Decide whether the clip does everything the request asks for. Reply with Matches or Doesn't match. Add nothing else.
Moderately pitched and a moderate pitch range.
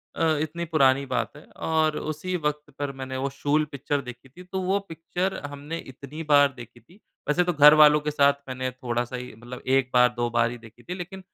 Matches